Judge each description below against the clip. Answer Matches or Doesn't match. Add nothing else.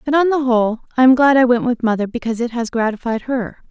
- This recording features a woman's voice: Matches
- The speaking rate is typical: Doesn't match